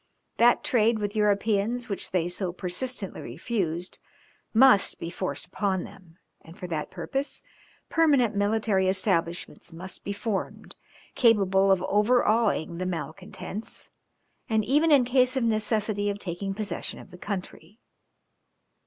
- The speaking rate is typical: No, slow, 130 wpm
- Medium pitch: No, high, 205 Hz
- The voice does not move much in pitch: No, average, 3.7 semitones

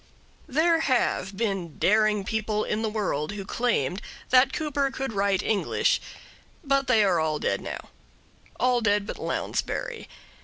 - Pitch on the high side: Yes, high, 215 Hz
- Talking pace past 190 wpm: No, average, 145 wpm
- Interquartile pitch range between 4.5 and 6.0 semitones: Yes, average, 4.9 semitones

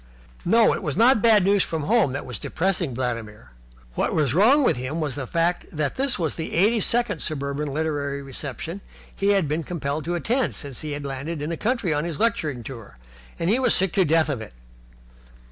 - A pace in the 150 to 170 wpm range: No, fast, 205 wpm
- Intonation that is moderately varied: No, wide, 6.0 semitones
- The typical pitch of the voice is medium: Yes, medium, 160 Hz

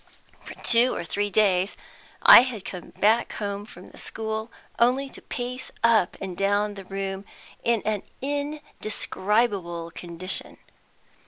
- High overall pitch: Yes, high, 210 Hz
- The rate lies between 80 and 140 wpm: Yes, slow, 135 wpm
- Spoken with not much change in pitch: No, average, 3.4 semitones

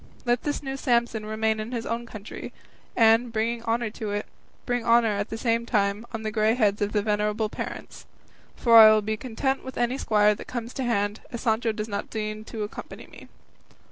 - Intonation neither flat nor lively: No, narrow, 1.9 semitones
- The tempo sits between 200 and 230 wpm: Yes, fast, 205 wpm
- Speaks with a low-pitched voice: No, high, 225 Hz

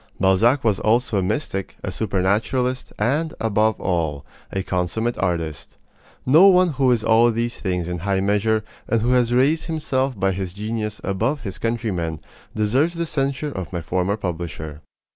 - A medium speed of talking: Yes, average, 160 wpm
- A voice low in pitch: Yes, low, 110 Hz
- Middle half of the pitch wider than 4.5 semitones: Yes, average, 5.1 semitones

